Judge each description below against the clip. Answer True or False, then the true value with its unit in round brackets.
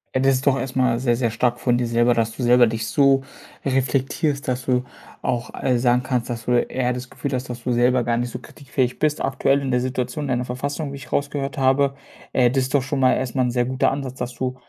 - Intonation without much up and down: True (1.8 semitones)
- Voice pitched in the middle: False (125 Hz)